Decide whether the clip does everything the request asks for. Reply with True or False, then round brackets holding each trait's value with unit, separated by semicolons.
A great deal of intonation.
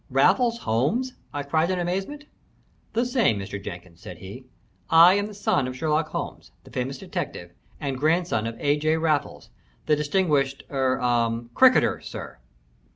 True (6.7 semitones)